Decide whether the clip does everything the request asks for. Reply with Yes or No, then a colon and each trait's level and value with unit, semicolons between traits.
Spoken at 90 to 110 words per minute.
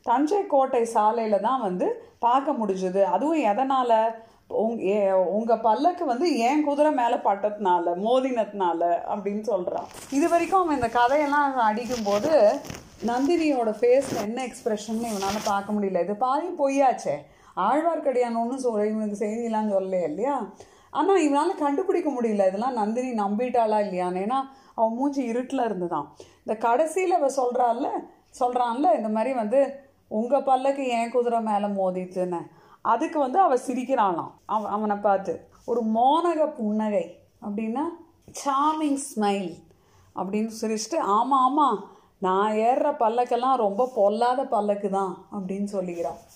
No: average, 125 wpm